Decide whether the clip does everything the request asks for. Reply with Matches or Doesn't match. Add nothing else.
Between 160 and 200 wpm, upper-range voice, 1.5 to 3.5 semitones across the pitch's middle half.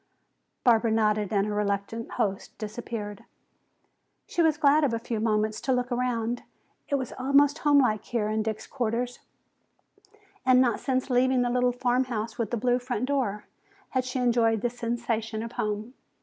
Matches